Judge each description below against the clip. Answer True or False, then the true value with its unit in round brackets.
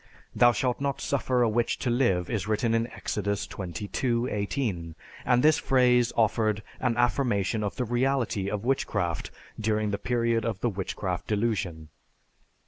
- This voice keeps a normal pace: True (150 wpm)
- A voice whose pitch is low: True (115 Hz)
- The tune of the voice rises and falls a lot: False (3.2 semitones)